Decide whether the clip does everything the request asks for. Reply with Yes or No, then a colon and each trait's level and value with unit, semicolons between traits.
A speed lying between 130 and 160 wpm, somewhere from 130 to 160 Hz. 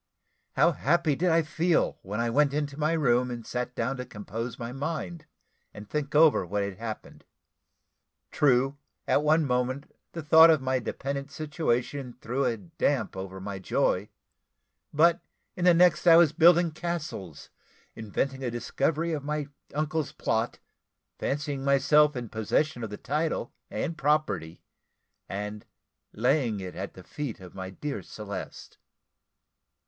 Yes: average, 150 wpm; medium, 140 Hz